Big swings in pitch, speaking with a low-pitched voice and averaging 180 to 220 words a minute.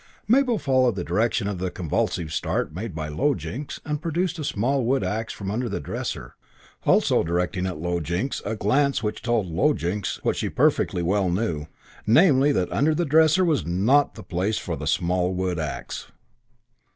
Yes: wide, 7.8 semitones; low, 105 Hz; average, 185 wpm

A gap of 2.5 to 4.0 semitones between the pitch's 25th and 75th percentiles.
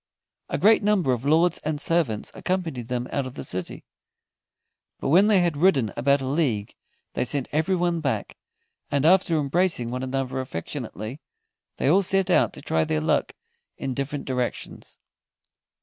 No: wide, 5.5 semitones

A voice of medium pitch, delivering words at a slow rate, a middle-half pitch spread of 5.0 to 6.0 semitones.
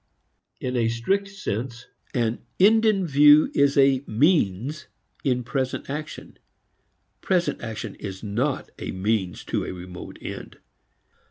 No: low, 130 Hz; slow, 125 wpm; average, 5.3 semitones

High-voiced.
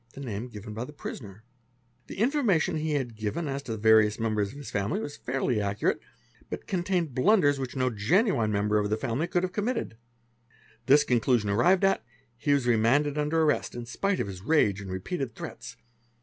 No: low, 125 Hz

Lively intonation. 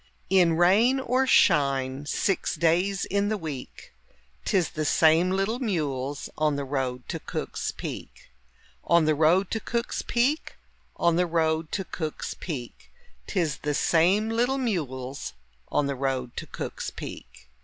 Yes: wide, 5.8 semitones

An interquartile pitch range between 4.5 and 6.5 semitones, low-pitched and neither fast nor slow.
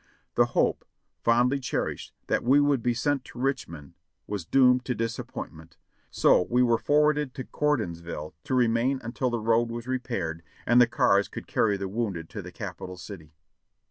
Yes: average, 4.9 semitones; low, 120 Hz; average, 175 wpm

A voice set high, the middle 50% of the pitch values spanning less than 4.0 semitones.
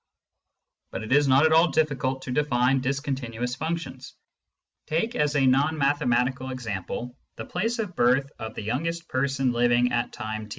No: low, 130 Hz; average, 3.4 semitones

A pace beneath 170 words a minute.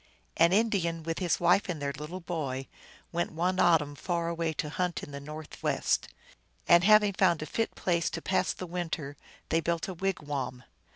No: average, 180 wpm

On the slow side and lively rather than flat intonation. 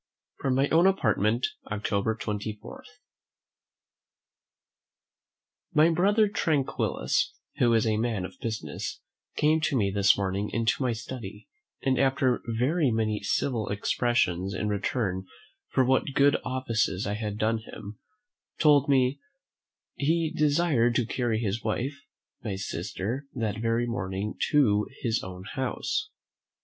No: slow, 125 wpm; average, 4.6 semitones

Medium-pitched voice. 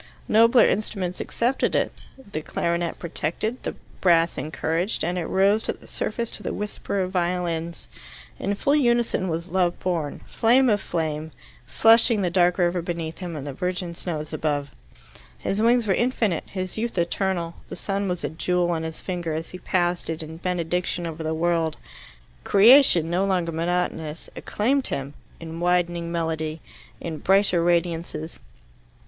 Yes: medium, 175 Hz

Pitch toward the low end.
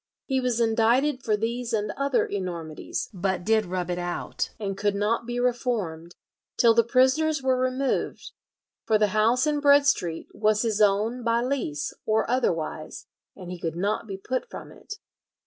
No: high, 225 Hz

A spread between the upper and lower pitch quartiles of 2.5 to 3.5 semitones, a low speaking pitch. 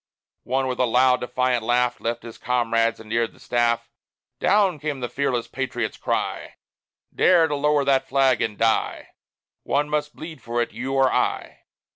Yes: average, 3.0 semitones; low, 125 Hz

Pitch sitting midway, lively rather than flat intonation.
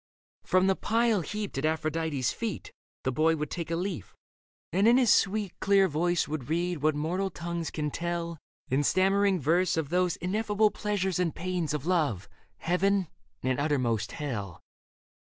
No: medium, 170 Hz; average, 4.1 semitones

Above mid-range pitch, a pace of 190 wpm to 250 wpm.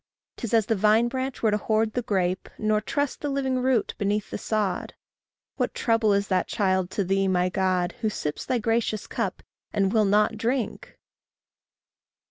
No: high, 215 Hz; average, 175 wpm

